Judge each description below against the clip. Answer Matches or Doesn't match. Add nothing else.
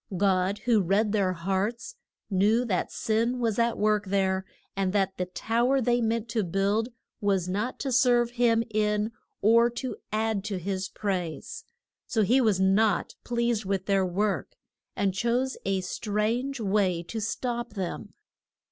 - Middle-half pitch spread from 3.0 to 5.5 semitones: Matches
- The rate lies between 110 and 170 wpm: Matches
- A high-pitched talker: Matches